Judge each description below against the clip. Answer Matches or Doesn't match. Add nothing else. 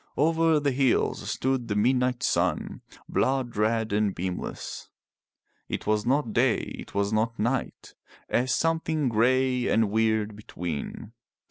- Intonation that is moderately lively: Matches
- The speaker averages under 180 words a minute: Matches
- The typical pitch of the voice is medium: Doesn't match